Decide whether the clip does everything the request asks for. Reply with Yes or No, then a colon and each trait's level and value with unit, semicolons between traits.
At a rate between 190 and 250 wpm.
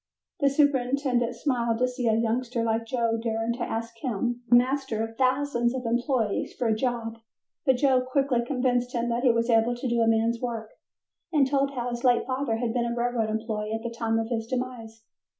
Yes: fast, 205 wpm